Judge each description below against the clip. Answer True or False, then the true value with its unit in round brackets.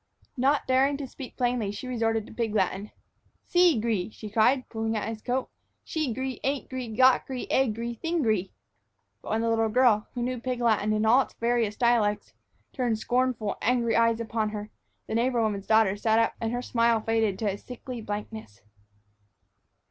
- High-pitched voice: True (230 Hz)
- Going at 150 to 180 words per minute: True (170 wpm)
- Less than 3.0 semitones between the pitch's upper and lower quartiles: True (2.6 semitones)